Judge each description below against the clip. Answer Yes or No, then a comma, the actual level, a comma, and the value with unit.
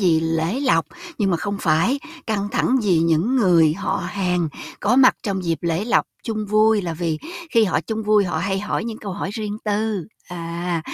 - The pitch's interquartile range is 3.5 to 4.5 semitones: Yes, average, 4.2 semitones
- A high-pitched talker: Yes, high, 195 Hz